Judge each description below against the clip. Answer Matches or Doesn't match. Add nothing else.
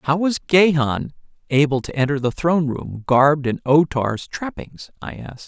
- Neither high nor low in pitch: Matches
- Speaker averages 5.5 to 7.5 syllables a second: Doesn't match